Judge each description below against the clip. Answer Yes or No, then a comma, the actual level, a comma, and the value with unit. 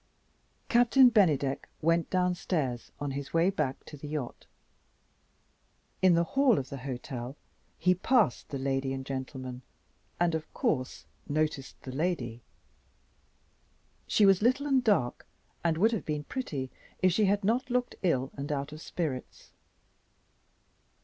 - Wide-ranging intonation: Yes, wide, 6.4 semitones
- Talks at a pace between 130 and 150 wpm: Yes, average, 140 wpm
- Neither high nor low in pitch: Yes, medium, 155 Hz